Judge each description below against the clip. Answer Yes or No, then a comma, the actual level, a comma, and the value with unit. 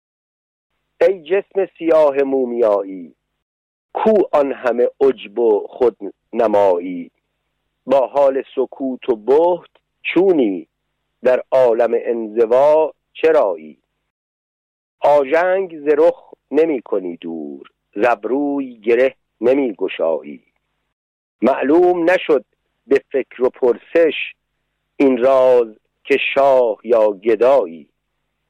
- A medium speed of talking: No, slow, 85 wpm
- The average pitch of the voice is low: No, medium, 170 Hz